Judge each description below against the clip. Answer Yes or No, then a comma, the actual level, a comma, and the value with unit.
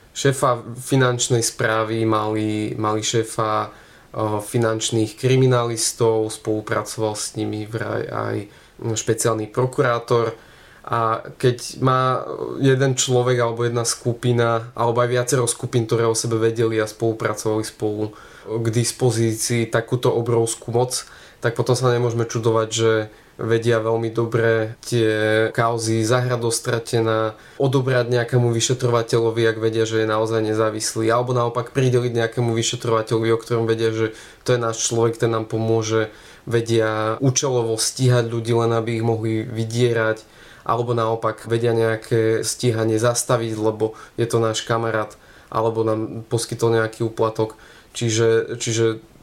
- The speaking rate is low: No, average, 125 wpm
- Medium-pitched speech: No, low, 115 Hz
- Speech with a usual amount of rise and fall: No, narrow, 1.3 semitones